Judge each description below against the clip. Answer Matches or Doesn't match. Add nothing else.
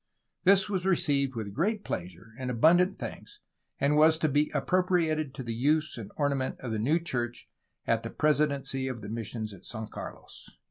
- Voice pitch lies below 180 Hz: Matches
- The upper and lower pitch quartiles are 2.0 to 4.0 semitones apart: Doesn't match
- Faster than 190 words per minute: Doesn't match